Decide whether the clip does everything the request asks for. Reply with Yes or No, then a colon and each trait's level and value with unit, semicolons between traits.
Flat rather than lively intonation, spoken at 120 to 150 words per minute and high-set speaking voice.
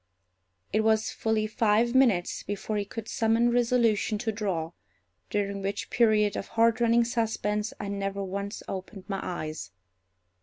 Yes: narrow, 2.3 semitones; average, 140 wpm; high, 215 Hz